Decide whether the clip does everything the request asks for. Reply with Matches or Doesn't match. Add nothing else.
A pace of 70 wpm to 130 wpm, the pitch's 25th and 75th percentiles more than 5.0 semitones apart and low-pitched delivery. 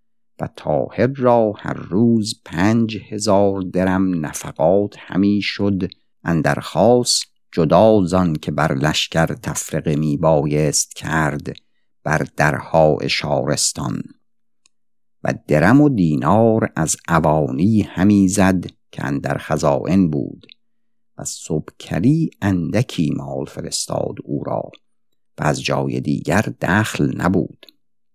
Matches